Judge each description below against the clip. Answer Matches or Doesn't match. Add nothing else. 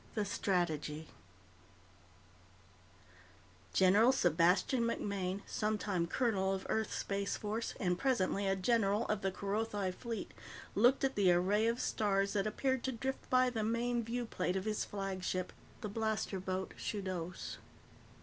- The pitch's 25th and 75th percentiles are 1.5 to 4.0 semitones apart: Matches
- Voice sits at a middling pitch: Doesn't match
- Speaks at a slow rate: Matches